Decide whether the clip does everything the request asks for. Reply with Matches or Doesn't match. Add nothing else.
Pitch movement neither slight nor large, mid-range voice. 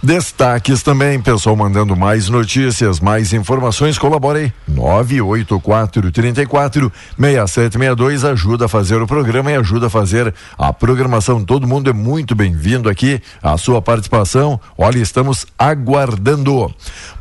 Doesn't match